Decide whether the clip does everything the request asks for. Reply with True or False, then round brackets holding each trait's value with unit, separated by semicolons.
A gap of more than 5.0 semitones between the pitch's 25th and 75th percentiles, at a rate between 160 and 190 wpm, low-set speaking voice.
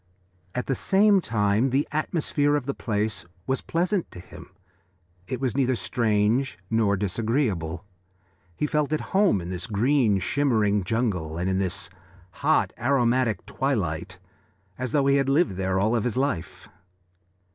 False (5.6 semitones; 145 wpm; 115 Hz)